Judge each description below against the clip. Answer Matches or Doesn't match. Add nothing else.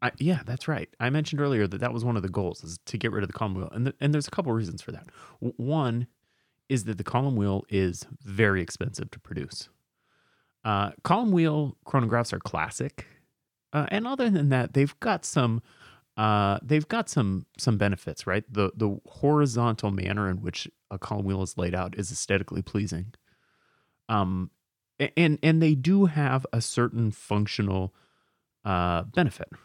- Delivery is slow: Doesn't match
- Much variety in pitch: Matches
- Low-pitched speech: Matches